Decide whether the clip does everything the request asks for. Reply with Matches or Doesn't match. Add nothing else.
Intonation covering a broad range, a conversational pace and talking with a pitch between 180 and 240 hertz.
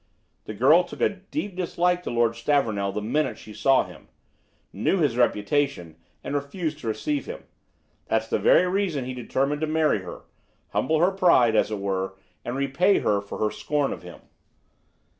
Doesn't match